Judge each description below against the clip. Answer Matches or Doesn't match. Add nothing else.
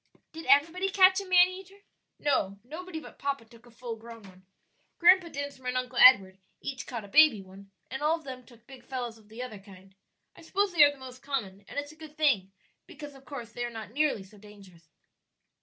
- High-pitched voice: Matches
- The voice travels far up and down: Matches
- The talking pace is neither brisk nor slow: Doesn't match